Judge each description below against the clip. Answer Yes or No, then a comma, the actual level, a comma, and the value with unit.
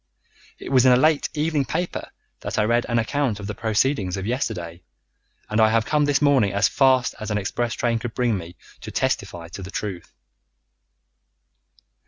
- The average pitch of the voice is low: Yes, low, 115 Hz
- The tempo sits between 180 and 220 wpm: Yes, average, 185 wpm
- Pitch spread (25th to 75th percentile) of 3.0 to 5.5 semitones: Yes, average, 4.8 semitones